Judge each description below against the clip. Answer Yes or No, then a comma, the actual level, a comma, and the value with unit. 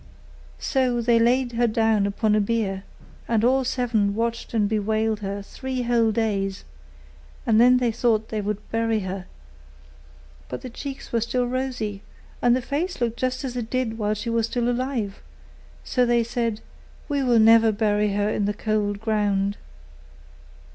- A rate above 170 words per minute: No, average, 160 wpm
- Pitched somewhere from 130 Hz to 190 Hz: No, high, 225 Hz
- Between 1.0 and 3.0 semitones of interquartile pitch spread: Yes, narrow, 2.6 semitones